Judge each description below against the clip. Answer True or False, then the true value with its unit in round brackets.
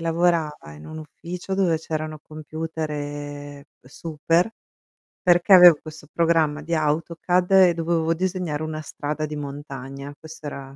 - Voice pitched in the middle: True (155 Hz)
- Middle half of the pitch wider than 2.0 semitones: True (2.4 semitones)